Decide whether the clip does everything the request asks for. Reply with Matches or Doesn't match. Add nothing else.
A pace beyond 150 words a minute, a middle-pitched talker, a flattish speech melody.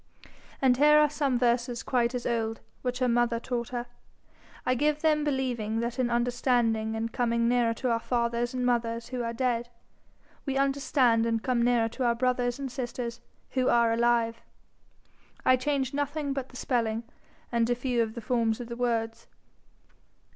Doesn't match